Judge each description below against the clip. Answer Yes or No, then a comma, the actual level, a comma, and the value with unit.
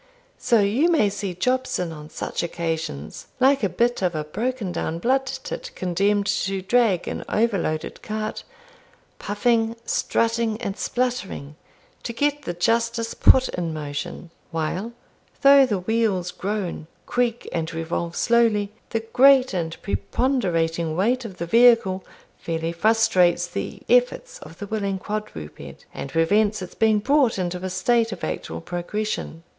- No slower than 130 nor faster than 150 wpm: Yes, average, 140 wpm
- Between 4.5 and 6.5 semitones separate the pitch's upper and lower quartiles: Yes, average, 5.2 semitones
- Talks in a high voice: Yes, high, 205 Hz